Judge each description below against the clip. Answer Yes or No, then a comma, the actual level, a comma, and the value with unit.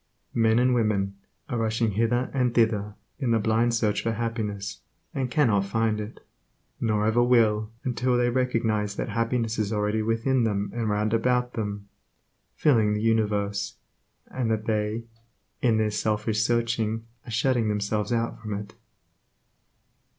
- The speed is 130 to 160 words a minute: Yes, average, 150 wpm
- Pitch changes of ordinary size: No, narrow, 1.9 semitones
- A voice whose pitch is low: Yes, low, 110 Hz